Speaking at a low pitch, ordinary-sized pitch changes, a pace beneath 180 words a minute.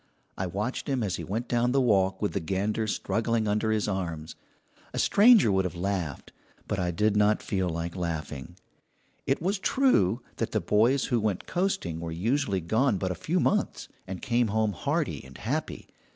No: low, 105 Hz; average, 4.6 semitones; average, 185 wpm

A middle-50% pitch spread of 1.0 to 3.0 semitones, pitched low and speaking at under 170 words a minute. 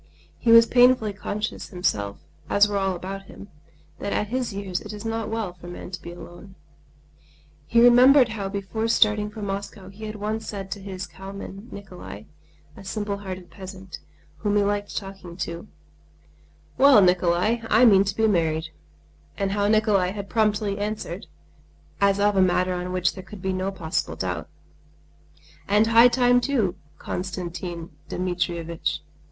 No: average, 2.7 semitones; high, 200 Hz; average, 160 wpm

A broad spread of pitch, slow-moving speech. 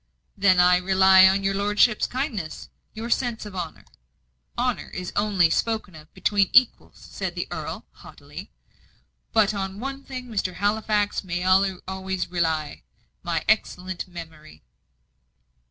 No: average, 3.0 semitones; slow, 130 wpm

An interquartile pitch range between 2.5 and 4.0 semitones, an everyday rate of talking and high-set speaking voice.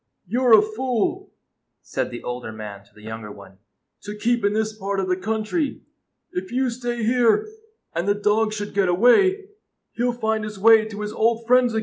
No: average, 3.7 semitones; fast, 210 wpm; high, 215 Hz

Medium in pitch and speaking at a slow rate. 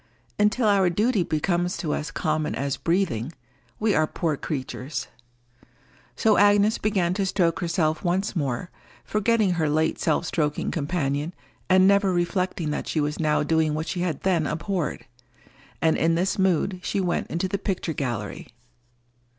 No: medium, 170 Hz; average, 155 wpm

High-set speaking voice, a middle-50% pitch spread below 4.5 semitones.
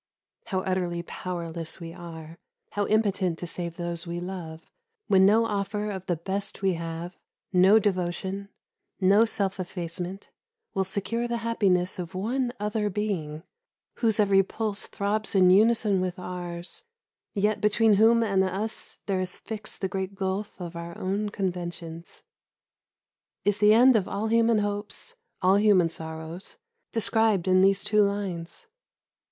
Yes: high, 195 Hz; average, 3.0 semitones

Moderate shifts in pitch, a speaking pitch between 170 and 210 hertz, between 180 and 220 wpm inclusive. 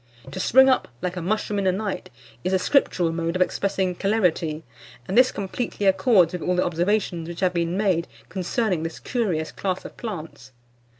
Yes: average, 3.5 semitones; medium, 185 Hz; average, 185 wpm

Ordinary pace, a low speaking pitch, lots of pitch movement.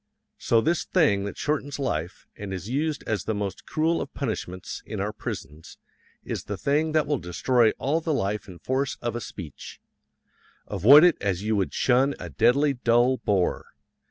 Yes: average, 180 wpm; low, 120 Hz; wide, 6.5 semitones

